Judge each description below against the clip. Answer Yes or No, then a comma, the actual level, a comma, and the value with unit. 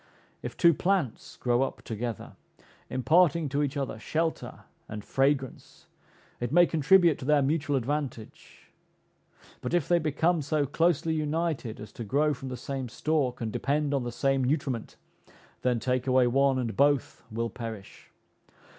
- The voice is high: No, medium, 140 Hz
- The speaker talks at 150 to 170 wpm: Yes, average, 155 wpm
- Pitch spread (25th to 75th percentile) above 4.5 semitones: No, average, 3.7 semitones